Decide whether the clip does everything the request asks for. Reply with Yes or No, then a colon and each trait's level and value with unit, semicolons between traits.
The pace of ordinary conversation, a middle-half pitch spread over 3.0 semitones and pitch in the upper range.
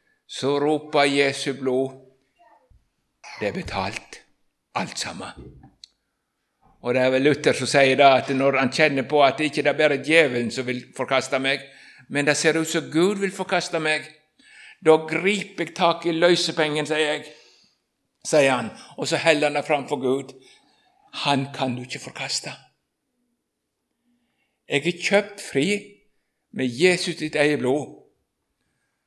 No: average, 150 wpm; average, 4.0 semitones; medium, 150 Hz